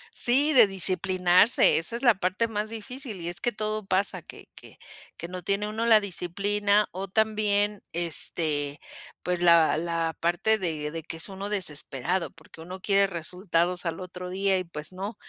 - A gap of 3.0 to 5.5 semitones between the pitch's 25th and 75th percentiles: Yes, average, 3.6 semitones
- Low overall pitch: No, medium, 185 Hz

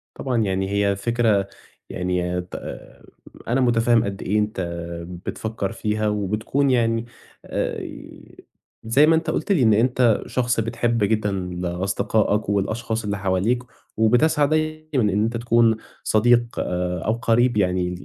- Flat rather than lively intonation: No, average, 3.3 semitones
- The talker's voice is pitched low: Yes, low, 110 Hz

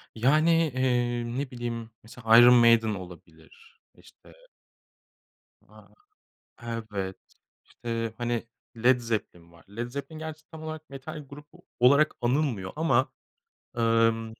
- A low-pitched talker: Yes, low, 120 Hz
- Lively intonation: No, average, 3.8 semitones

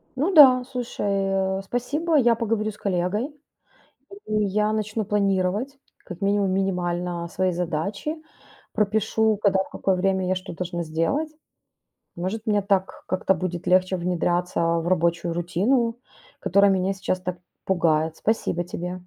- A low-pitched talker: No, high, 190 Hz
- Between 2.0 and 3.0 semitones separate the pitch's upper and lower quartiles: No, average, 3.4 semitones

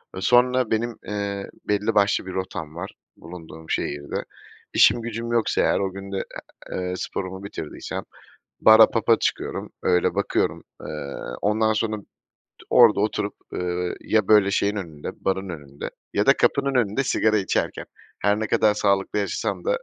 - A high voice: No, low, 100 Hz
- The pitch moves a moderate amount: Yes, average, 3.1 semitones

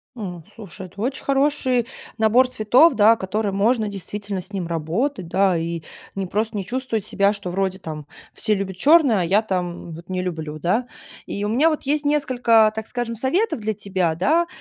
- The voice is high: Yes, high, 210 Hz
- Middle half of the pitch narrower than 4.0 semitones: No, average, 5.0 semitones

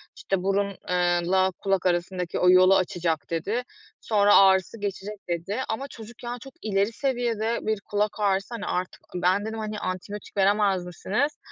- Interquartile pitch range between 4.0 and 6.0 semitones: No, average, 2.9 semitones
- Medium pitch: No, high, 200 Hz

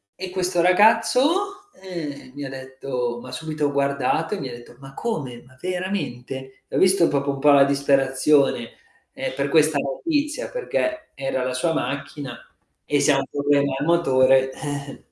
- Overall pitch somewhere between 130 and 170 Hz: Yes, medium, 140 Hz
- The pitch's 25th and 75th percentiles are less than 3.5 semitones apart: No, average, 5.0 semitones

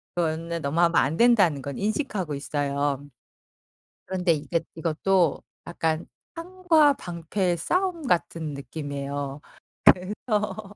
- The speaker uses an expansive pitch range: Yes, wide, 6.1 semitones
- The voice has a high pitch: No, medium, 170 Hz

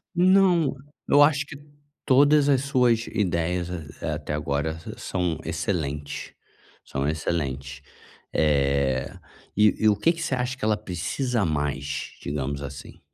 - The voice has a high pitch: No, very low, 90 Hz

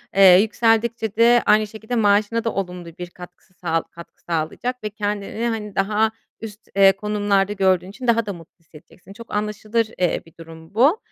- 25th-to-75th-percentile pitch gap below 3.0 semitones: No, average, 3.5 semitones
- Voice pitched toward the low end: No, high, 205 Hz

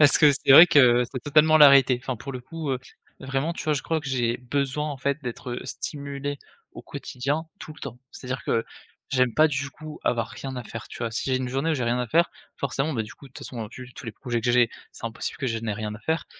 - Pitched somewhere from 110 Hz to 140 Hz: Yes, low, 135 Hz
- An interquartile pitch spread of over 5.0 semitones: No, average, 3.0 semitones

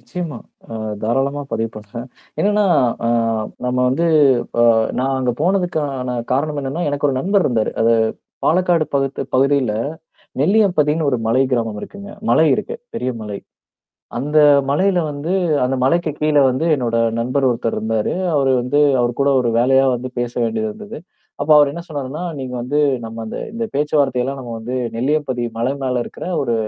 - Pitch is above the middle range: No, low, 135 Hz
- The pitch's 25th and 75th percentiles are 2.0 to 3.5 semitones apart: No, average, 4.1 semitones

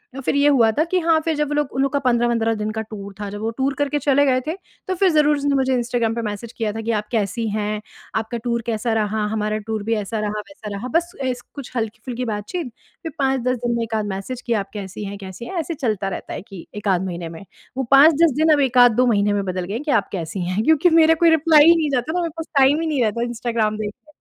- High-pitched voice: Yes, high, 235 Hz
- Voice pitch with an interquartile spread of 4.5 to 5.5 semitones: Yes, average, 5.2 semitones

